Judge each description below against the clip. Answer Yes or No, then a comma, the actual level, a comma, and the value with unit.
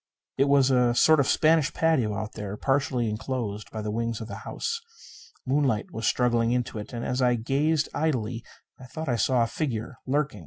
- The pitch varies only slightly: No, average, 3.9 semitones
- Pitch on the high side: No, low, 125 Hz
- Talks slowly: No, average, 195 wpm